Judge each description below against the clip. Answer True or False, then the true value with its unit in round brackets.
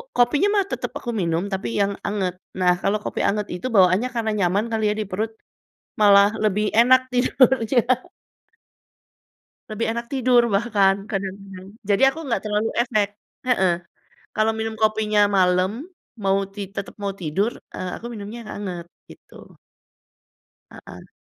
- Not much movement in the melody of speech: False (3.2 semitones)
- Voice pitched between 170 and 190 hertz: False (210 Hz)